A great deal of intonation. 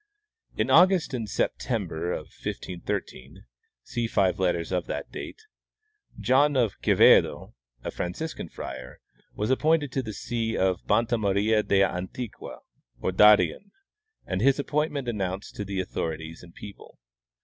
Yes: wide, 5.7 semitones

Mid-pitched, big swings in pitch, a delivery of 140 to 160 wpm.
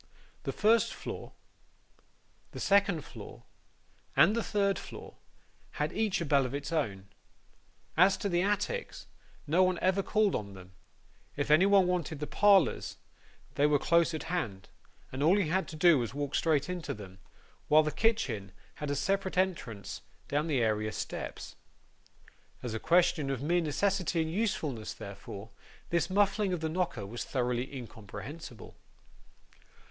Yes: medium, 160 Hz; wide, 6.5 semitones; average, 155 wpm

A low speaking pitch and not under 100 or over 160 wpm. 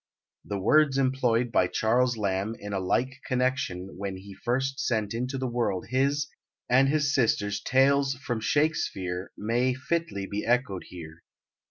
Yes: low, 120 Hz; average, 150 wpm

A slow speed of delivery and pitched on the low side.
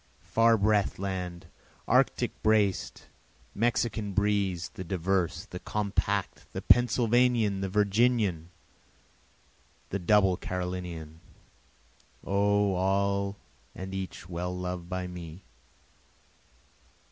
Yes: slow, 90 wpm; very low, 95 Hz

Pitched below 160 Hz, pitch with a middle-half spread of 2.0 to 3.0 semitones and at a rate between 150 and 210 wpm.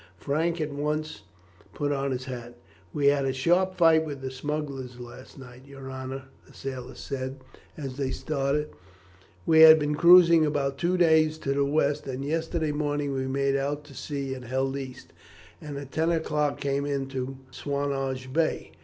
Yes: medium, 140 Hz; narrow, 2.4 semitones; average, 175 wpm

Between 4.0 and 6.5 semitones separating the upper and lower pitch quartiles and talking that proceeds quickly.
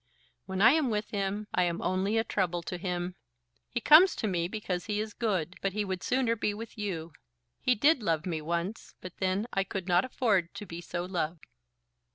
No: average, 3.5 semitones; fast, 210 wpm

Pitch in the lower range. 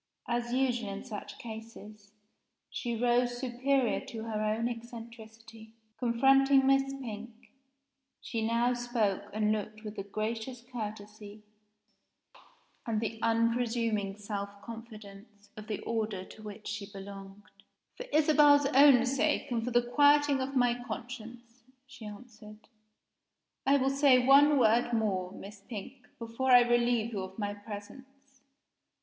No: high, 230 Hz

